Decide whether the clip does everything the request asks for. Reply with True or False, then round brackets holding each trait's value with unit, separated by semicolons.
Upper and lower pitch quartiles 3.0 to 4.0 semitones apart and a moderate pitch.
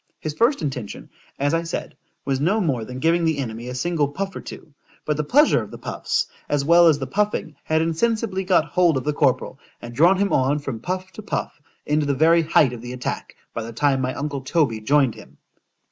False (4.4 semitones; 150 Hz)